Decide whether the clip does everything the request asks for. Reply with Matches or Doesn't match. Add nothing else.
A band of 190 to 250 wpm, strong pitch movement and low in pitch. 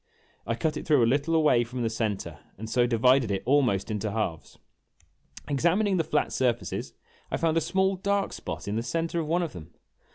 Matches